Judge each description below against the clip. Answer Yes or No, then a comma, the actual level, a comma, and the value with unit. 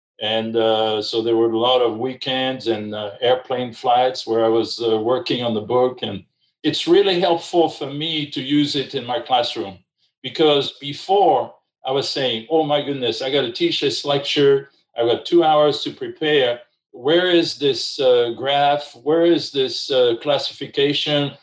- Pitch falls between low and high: Yes, medium, 145 Hz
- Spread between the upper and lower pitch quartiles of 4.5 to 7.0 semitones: Yes, wide, 5.5 semitones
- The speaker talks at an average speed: Yes, average, 175 wpm